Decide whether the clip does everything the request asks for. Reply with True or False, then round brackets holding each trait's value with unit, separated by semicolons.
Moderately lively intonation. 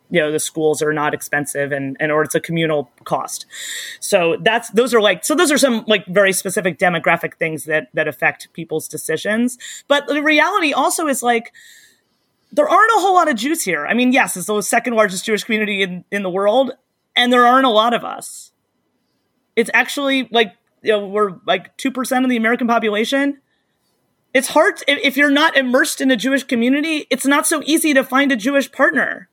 False (6.8 semitones)